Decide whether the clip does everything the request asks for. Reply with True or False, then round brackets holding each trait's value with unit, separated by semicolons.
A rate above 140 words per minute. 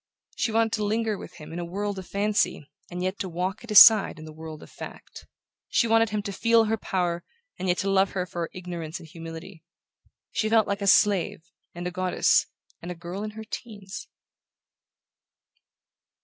True (200 wpm)